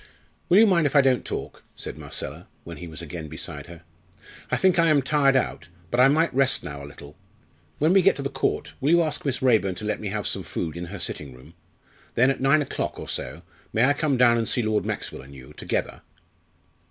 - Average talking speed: No, fast, 235 wpm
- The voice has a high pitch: No, low, 120 Hz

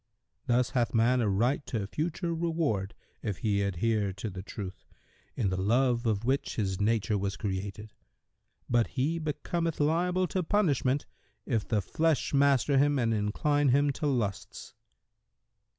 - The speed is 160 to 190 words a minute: No, average, 150 wpm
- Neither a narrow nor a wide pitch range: No, wide, 6.0 semitones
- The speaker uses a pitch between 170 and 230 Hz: No, low, 120 Hz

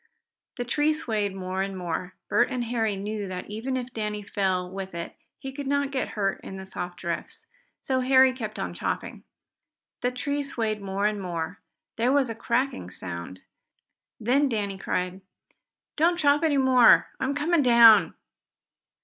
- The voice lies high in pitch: Yes, high, 220 Hz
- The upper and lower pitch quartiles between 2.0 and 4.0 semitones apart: No, wide, 5.5 semitones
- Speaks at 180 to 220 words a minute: No, average, 165 wpm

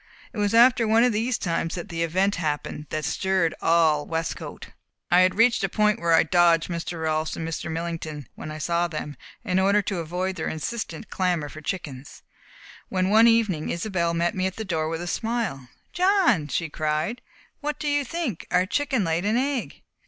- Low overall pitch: No, medium, 180 Hz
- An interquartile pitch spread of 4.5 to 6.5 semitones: Yes, average, 5.1 semitones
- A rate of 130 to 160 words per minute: No, average, 195 wpm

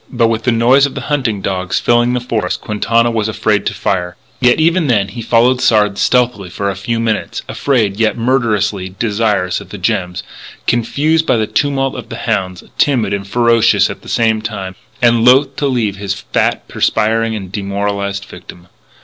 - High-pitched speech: No, low, 115 Hz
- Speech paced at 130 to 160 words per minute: No, average, 185 wpm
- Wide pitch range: No, average, 3.5 semitones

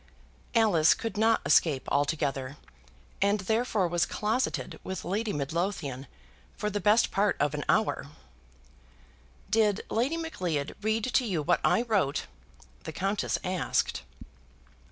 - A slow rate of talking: Yes, slow, 125 wpm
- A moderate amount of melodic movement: No, wide, 6.0 semitones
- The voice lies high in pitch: Yes, high, 195 Hz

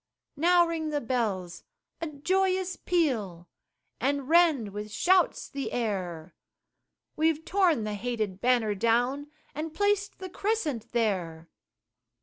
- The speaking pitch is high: Yes, very high, 265 Hz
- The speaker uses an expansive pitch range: Yes, wide, 8.1 semitones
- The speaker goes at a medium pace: No, slow, 120 wpm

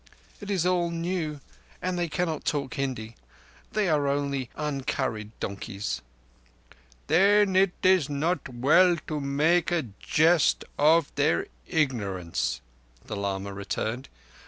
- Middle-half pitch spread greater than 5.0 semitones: Yes, wide, 5.5 semitones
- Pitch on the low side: No, medium, 150 Hz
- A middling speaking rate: No, slow, 120 wpm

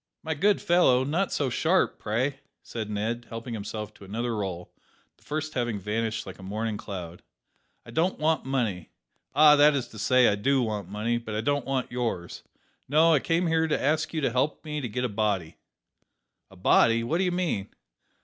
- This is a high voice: No, low, 120 Hz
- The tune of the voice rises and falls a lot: Yes, wide, 6.0 semitones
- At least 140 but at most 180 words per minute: No, average, 195 wpm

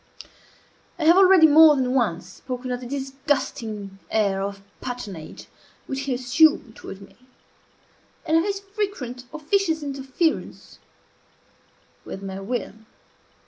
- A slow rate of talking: Yes, slow, 120 wpm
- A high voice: Yes, very high, 265 Hz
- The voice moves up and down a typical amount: No, wide, 6.5 semitones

